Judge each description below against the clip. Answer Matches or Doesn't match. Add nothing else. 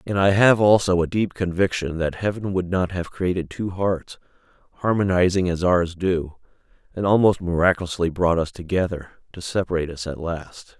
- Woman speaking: Doesn't match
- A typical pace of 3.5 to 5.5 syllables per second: Matches